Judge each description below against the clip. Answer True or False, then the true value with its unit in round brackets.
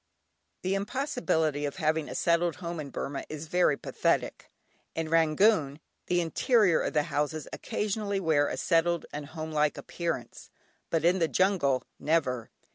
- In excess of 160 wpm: False (145 wpm)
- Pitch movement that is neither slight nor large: True (3.2 semitones)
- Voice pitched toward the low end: False (160 Hz)